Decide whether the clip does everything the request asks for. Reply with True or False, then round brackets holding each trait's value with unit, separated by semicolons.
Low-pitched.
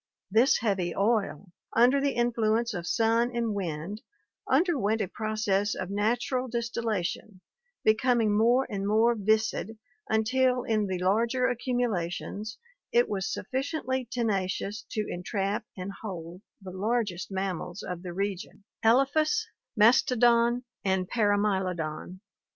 False (215 Hz)